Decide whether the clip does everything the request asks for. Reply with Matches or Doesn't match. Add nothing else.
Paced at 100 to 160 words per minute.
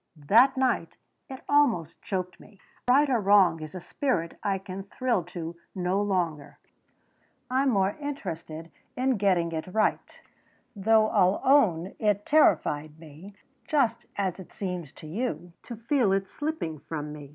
Matches